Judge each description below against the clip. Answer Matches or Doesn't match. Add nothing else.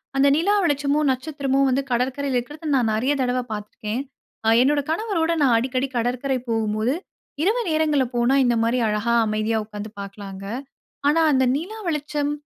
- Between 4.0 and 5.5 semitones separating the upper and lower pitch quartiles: Matches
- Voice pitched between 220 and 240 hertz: Doesn't match